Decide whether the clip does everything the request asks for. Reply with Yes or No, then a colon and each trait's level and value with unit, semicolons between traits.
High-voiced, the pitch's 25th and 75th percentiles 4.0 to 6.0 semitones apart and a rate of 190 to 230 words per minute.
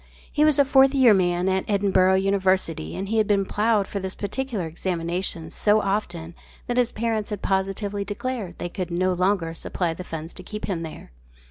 No: high, 195 Hz; average, 3.1 semitones; average, 195 wpm